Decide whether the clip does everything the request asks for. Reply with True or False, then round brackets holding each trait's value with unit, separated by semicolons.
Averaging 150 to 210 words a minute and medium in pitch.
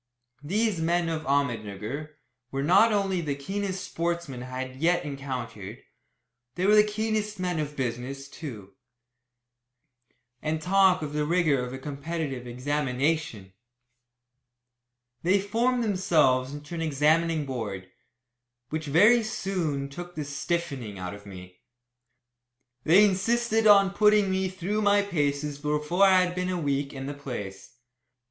False (135 wpm; 155 Hz)